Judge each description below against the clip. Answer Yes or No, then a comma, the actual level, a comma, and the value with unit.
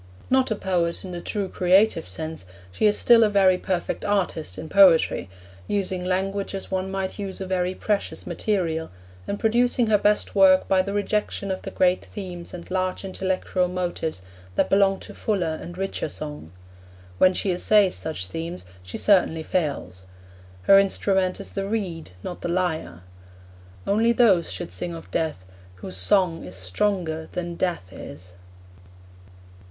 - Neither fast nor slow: Yes, average, 160 wpm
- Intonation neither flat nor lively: Yes, average, 3.4 semitones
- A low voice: No, medium, 185 Hz